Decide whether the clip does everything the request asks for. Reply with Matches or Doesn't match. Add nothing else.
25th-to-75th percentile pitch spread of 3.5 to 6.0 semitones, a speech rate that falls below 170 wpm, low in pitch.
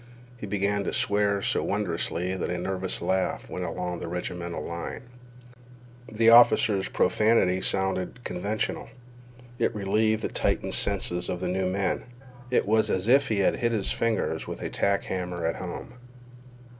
Doesn't match